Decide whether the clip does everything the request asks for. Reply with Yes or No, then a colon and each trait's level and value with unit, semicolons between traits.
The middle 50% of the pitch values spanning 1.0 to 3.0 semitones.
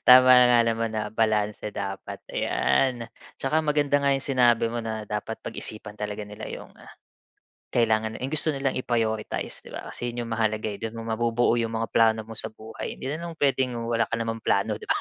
Yes: narrow, 2.5 semitones